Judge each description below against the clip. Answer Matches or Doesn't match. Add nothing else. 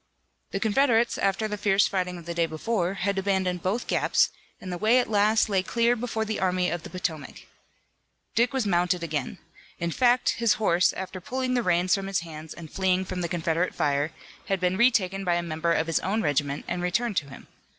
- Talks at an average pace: Doesn't match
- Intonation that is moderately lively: Matches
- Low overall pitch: Doesn't match